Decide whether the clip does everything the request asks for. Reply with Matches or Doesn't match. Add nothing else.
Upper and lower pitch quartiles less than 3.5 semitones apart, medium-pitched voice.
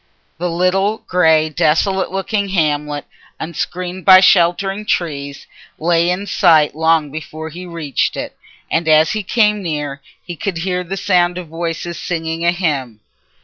Matches